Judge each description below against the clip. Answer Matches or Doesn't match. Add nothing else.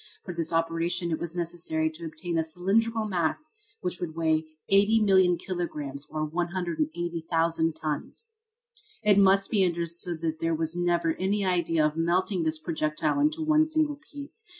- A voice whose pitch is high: Doesn't match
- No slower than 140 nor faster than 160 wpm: Matches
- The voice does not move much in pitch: Doesn't match